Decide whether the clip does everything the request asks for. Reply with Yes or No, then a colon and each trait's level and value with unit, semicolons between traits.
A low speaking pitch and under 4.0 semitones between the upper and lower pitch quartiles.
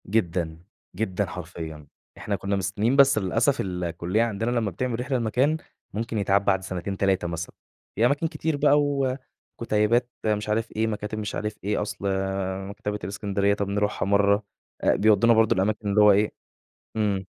Yes: low, 105 Hz; average, 2.9 semitones